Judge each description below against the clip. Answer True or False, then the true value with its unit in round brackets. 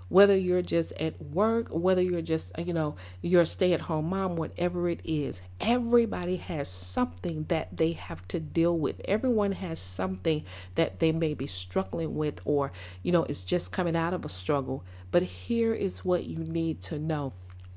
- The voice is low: False (165 Hz)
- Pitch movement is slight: False (3.9 semitones)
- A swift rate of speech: False (180 wpm)